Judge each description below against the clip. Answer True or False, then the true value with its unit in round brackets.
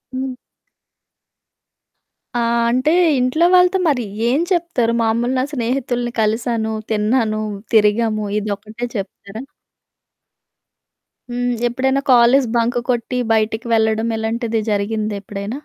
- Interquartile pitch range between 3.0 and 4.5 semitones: False (2.6 semitones)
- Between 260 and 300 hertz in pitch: False (235 Hz)